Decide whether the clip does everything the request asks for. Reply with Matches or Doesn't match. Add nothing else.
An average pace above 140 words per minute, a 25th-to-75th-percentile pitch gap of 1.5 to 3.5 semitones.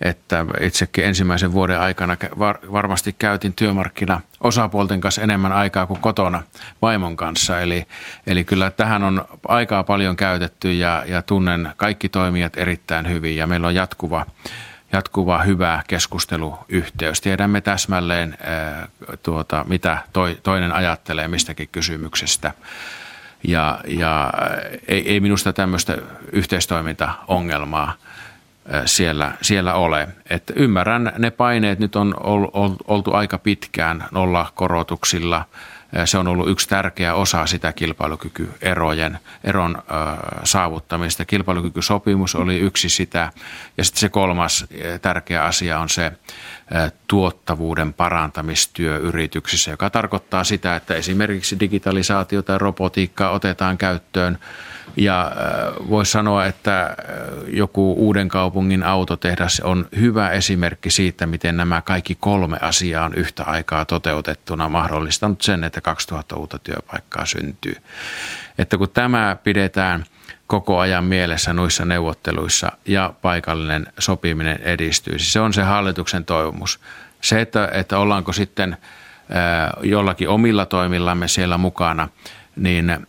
Doesn't match